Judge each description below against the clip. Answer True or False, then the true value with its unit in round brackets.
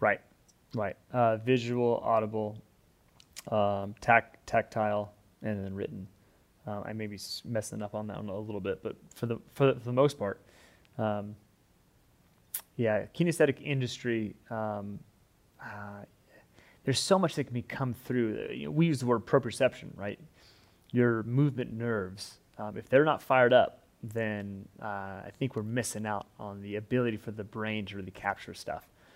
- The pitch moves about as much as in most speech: True (3.1 semitones)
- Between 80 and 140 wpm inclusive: False (165 wpm)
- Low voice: True (110 Hz)